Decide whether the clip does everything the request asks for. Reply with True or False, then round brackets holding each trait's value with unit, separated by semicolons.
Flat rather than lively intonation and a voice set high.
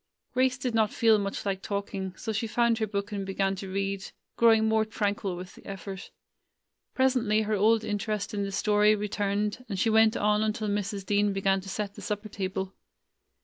True (1.8 semitones; 205 Hz)